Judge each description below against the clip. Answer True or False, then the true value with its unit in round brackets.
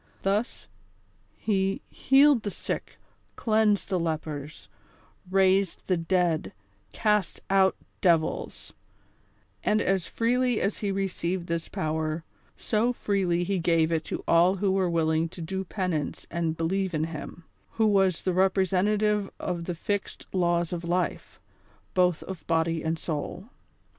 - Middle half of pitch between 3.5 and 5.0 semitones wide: False (3.0 semitones)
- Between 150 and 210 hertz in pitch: True (185 Hz)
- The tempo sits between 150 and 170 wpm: False (135 wpm)